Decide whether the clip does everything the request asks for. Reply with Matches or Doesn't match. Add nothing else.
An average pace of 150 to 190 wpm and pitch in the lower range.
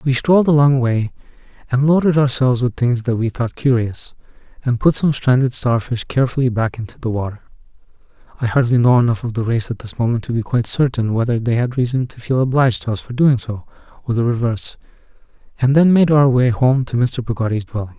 Doesn't match